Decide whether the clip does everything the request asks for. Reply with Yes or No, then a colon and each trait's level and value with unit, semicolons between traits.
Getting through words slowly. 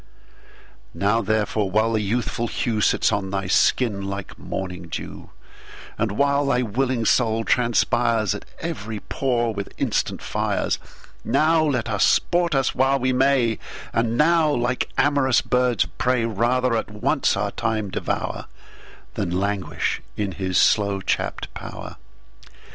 Yes: slow, 120 wpm